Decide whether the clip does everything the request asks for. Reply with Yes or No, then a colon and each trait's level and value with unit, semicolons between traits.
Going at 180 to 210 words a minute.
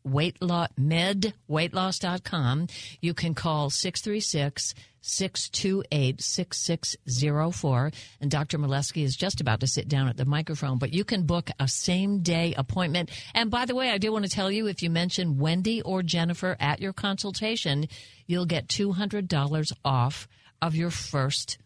No: average, 145 wpm